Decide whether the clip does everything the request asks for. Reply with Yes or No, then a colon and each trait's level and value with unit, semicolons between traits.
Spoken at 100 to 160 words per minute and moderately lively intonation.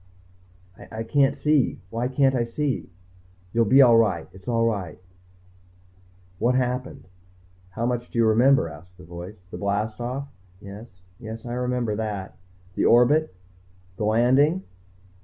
Yes: average, 140 wpm; average, 3.5 semitones